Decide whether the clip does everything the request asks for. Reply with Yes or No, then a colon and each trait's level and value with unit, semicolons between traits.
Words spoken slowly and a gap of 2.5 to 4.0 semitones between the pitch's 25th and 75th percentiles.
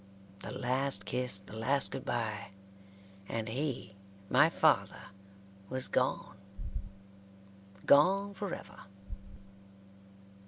No: slow, 85 wpm; average, 5.0 semitones